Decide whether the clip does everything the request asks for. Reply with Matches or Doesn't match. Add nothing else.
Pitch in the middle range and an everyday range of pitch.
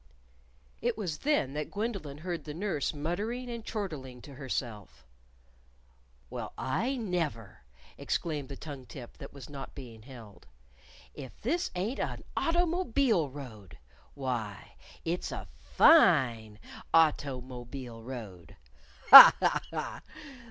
Doesn't match